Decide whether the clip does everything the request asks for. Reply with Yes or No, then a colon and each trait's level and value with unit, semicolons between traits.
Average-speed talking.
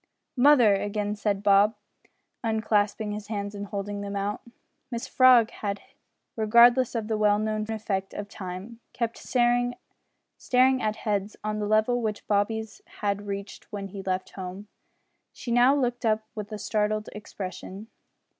Yes: average, 150 wpm